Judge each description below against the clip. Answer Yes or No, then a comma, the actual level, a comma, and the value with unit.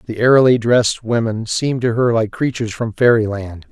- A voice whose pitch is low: Yes, low, 115 Hz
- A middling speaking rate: Yes, average, 195 wpm